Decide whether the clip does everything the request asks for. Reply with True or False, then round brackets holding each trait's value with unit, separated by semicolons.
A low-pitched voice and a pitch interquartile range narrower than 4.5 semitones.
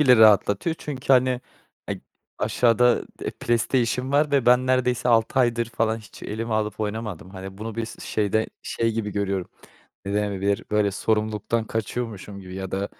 True (110 Hz; 3.0 semitones)